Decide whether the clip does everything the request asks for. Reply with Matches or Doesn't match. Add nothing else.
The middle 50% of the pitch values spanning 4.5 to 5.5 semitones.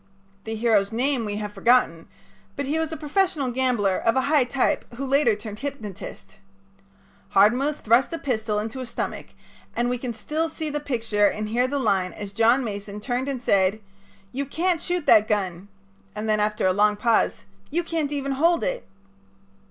Matches